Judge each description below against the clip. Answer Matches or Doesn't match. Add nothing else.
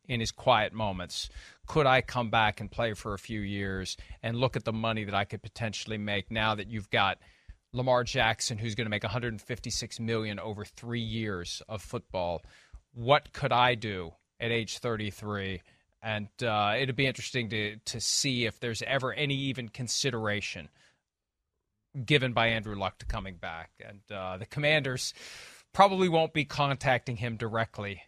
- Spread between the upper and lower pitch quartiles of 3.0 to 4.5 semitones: Matches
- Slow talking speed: Doesn't match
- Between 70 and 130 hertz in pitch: Matches